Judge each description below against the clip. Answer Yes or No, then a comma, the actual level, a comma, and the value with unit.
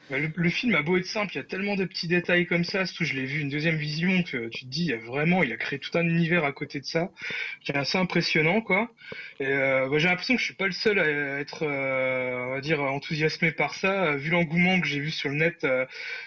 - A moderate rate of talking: No, fast, 275 wpm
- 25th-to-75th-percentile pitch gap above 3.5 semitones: Yes, average, 4.2 semitones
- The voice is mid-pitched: Yes, medium, 165 Hz